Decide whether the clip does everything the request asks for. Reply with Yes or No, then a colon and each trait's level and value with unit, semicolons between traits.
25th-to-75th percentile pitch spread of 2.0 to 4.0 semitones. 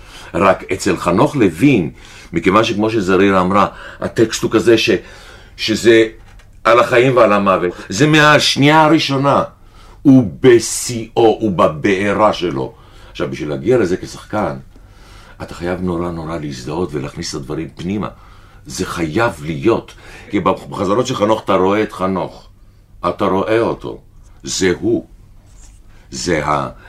Yes: average, 3.2 semitones